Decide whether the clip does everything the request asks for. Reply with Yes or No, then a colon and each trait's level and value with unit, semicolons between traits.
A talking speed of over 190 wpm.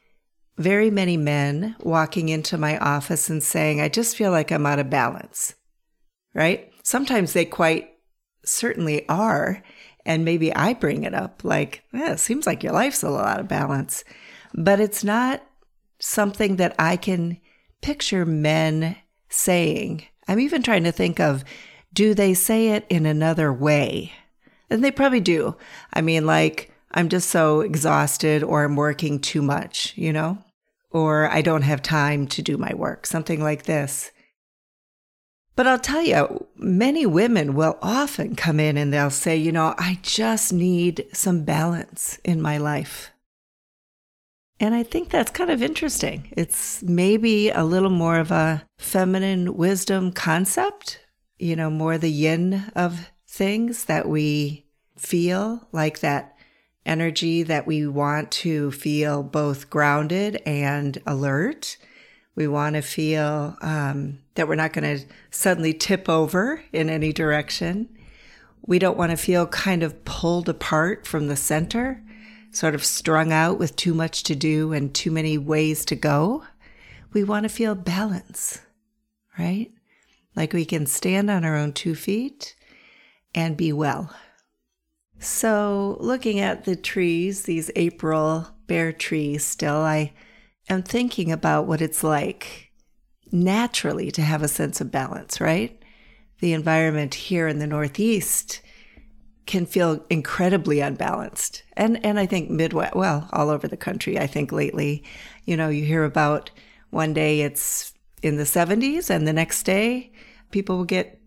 No: average, 155 wpm